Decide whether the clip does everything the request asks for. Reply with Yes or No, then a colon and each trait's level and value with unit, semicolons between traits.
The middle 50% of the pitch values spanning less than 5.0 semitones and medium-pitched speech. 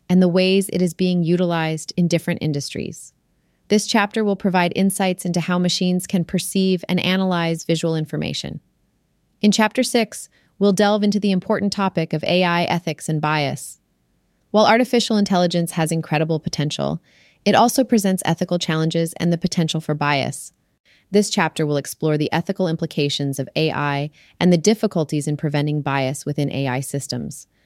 Yes: average, 3.8 semitones; medium, 175 Hz